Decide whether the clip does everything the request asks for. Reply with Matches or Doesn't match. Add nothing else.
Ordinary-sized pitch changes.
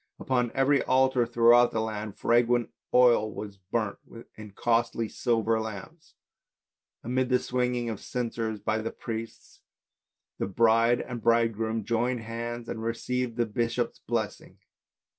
Doesn't match